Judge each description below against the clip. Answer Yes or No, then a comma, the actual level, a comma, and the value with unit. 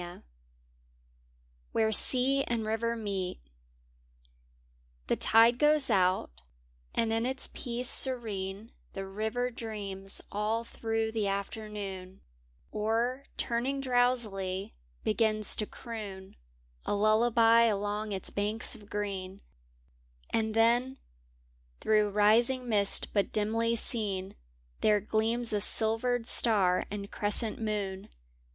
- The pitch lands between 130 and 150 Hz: No, high, 220 Hz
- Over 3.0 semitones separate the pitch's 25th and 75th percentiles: No, narrow, 2.5 semitones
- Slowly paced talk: Yes, slow, 105 wpm